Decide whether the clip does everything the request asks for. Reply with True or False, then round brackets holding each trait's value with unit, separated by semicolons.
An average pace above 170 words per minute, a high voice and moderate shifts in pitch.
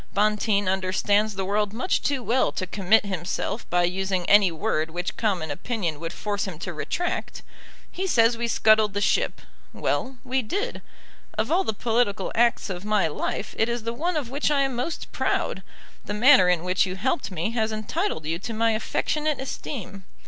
True (185 wpm; 215 Hz; 4.6 semitones)